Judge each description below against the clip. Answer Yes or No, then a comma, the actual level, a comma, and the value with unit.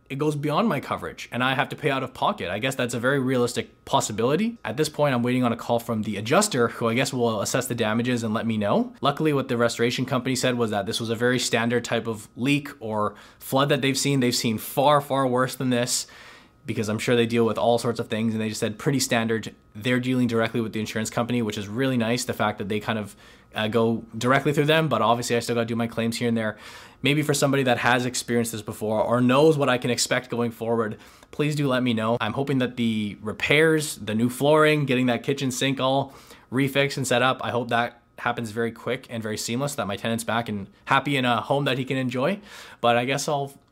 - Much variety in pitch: No, average, 2.8 semitones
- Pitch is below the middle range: Yes, low, 120 Hz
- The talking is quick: Yes, fast, 255 wpm